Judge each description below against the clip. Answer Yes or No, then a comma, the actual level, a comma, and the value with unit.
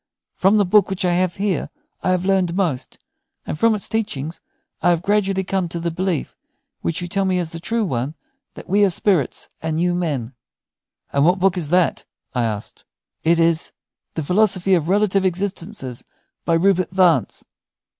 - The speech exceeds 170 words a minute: Yes, average, 180 wpm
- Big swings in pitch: No, average, 2.8 semitones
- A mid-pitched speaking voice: Yes, medium, 180 Hz